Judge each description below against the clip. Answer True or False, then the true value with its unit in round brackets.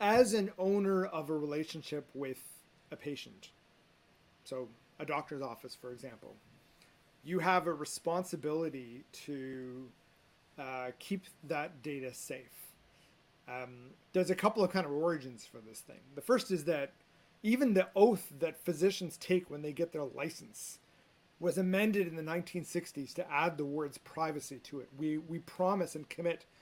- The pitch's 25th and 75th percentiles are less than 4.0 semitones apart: False (4.3 semitones)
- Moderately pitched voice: True (160 Hz)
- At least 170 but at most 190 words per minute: False (155 wpm)